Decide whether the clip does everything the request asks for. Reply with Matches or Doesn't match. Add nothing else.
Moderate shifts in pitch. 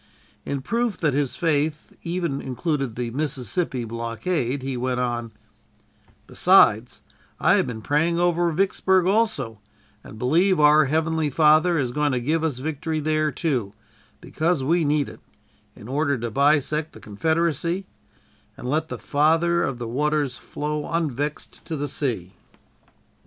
Matches